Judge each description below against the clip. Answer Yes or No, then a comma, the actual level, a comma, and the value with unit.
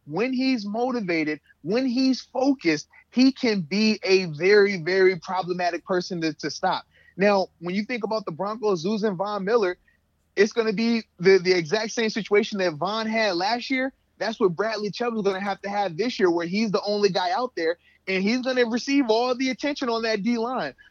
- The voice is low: No, high, 205 Hz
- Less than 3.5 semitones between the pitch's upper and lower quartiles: No, average, 4.0 semitones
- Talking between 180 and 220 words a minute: Yes, fast, 205 wpm